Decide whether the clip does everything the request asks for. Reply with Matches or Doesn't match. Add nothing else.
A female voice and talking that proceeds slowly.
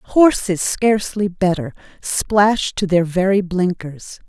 Matches